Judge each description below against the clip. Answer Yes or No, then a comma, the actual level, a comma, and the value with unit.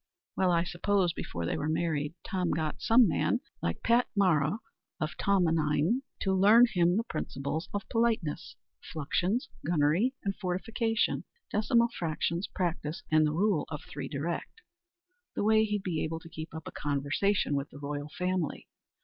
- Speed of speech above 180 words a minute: No, average, 160 wpm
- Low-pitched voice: No, medium, 175 Hz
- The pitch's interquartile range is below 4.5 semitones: No, average, 4.9 semitones